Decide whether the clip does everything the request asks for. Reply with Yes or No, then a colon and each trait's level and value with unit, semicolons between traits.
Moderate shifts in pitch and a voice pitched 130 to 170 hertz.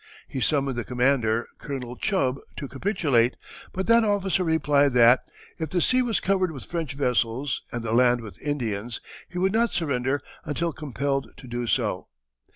No: wide, 5.7 semitones; medium, 140 Hz